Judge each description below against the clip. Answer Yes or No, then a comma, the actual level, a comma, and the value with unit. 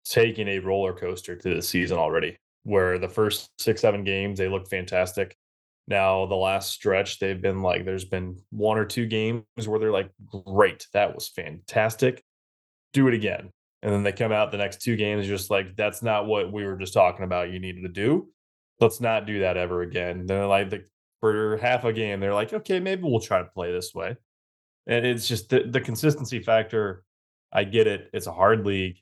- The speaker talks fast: Yes, fast, 210 wpm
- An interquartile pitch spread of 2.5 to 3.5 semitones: Yes, average, 2.9 semitones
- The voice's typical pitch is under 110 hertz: Yes, low, 100 Hz